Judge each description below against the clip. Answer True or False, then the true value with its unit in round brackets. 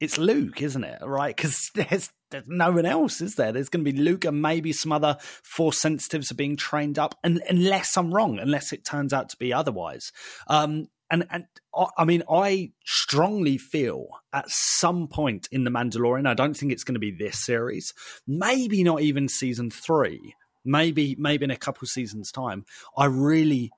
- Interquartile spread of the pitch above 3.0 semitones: True (3.8 semitones)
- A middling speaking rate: True (190 wpm)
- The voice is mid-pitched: True (145 Hz)